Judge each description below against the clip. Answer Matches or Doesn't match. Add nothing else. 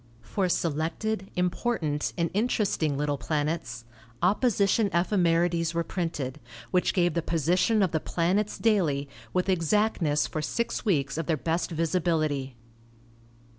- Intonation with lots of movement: Doesn't match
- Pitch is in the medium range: Matches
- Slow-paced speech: Matches